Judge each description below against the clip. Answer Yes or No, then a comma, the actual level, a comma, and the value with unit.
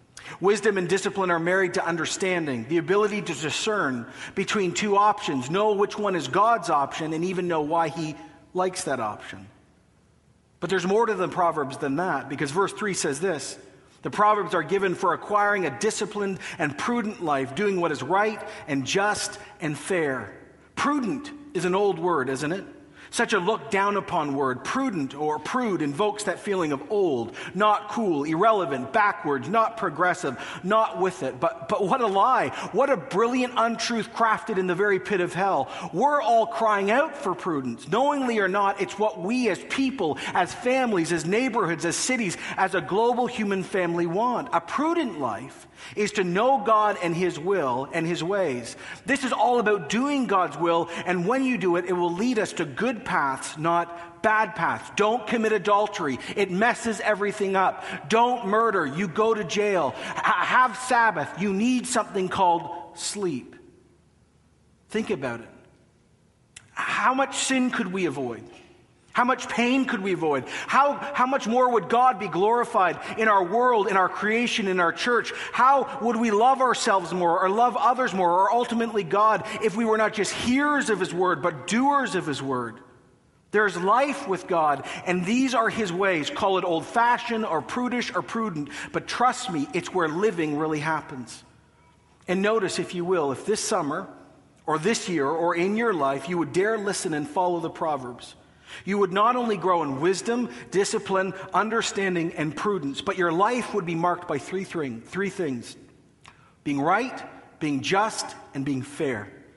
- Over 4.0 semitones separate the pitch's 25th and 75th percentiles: Yes, average, 4.7 semitones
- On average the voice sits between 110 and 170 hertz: No, high, 195 Hz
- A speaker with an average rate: Yes, average, 175 wpm